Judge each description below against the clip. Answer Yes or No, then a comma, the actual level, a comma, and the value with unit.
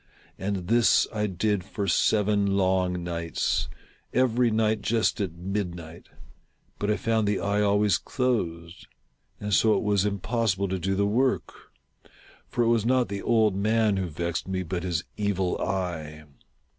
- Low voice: Yes, low, 100 Hz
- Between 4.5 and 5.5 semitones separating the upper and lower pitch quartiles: No, average, 3.2 semitones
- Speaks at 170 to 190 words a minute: No, average, 160 wpm